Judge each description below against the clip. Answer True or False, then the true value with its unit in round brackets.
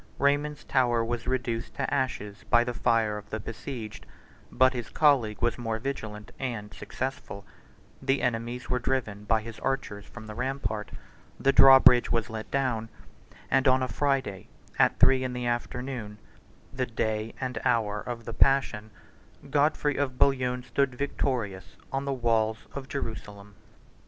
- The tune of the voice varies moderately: True (3.3 semitones)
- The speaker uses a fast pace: False (155 wpm)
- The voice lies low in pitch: True (120 Hz)